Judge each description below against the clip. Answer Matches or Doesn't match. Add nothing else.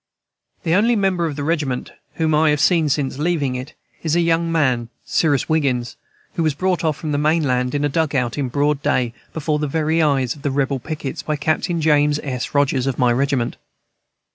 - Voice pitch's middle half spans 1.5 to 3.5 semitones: Matches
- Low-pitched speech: Doesn't match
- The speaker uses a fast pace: Matches